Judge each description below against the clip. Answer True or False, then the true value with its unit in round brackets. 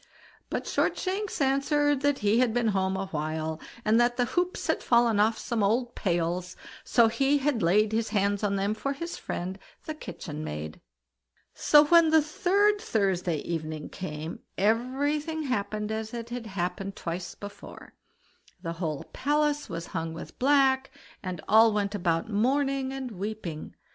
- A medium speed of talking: True (160 wpm)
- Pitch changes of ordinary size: False (6.8 semitones)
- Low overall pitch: False (220 Hz)